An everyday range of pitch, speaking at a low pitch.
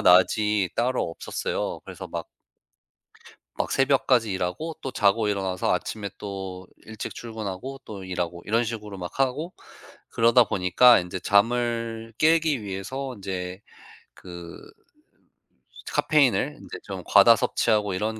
Yes: average, 4.4 semitones; low, 105 Hz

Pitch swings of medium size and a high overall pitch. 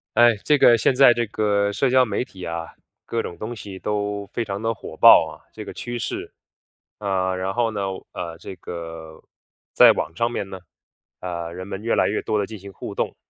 No: average, 3.7 semitones; low, 100 Hz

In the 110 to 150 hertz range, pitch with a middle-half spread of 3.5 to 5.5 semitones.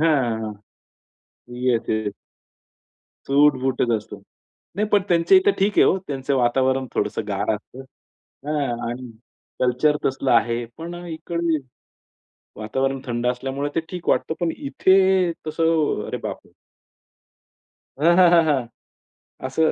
Yes: medium, 140 Hz; average, 5.1 semitones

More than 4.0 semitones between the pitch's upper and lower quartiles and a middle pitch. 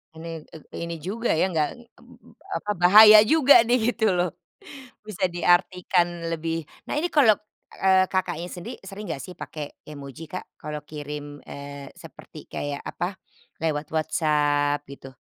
Yes: average, 4.5 semitones; medium, 170 Hz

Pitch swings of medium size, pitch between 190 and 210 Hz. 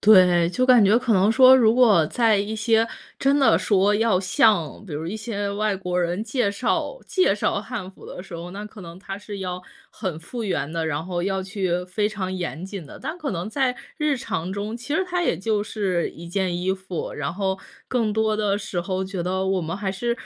Yes: average, 3.5 semitones; high, 200 Hz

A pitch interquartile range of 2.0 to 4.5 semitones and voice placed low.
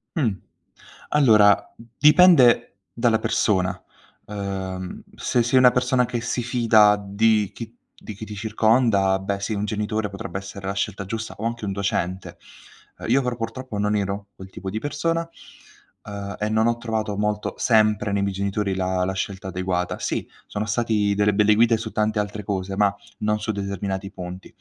Yes: narrow, 2.5 semitones; low, 105 Hz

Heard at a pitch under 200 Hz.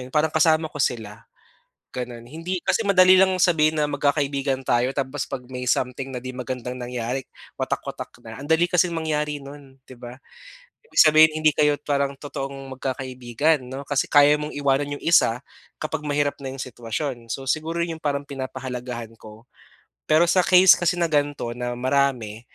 Yes: medium, 140 Hz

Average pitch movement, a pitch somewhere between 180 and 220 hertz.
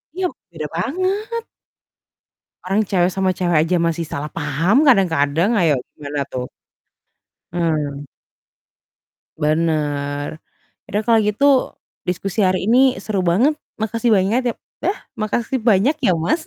No: wide, 6.7 semitones; medium, 185 Hz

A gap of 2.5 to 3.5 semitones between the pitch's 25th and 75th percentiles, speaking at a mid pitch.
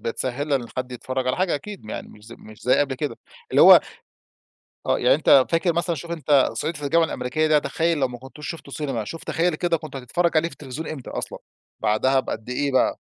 No: average, 4.3 semitones; medium, 145 Hz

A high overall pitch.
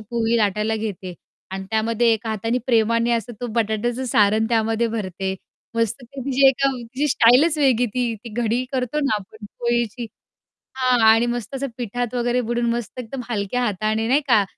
Yes: high, 235 Hz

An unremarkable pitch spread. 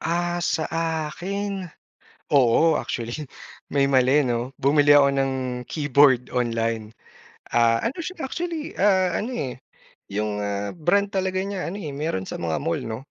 No: wide, 7.6 semitones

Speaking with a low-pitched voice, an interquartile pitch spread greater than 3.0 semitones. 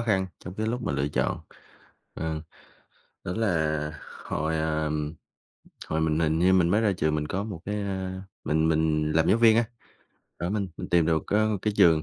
Yes: very low, 85 Hz; average, 4.4 semitones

